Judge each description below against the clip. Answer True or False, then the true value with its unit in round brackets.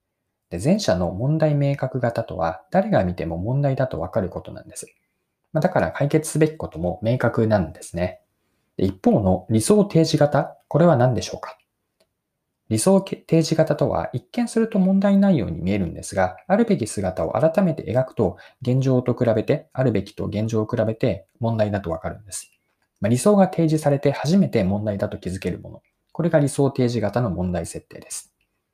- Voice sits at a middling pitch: False (120 Hz)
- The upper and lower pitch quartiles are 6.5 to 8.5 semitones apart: True (7.8 semitones)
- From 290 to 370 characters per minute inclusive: True (350 characters per minute)